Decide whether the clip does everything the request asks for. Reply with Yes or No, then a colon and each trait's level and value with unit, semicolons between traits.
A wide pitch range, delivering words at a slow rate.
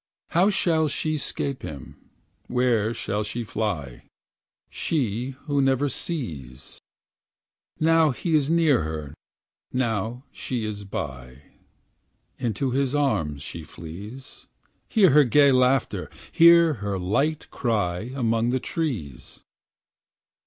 Yes: wide, 6.6 semitones; slow, 115 wpm